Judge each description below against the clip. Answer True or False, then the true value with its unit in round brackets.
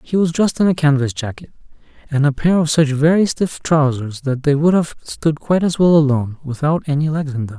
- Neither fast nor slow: False (230 wpm)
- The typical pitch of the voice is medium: True (150 Hz)